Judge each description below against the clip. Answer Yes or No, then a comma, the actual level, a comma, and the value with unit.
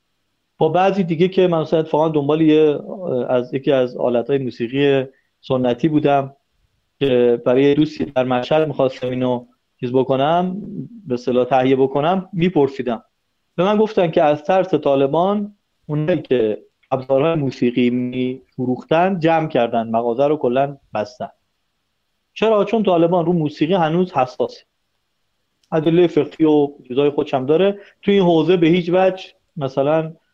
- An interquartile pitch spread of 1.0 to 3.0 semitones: No, average, 5.3 semitones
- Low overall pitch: No, medium, 150 Hz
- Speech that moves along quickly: No, average, 135 wpm